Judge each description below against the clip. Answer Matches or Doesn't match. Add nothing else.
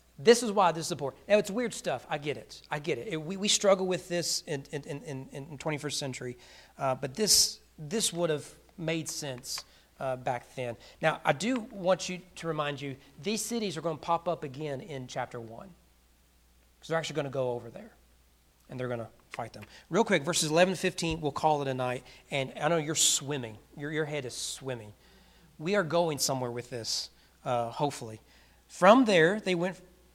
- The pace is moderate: Doesn't match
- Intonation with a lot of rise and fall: Matches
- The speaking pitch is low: Doesn't match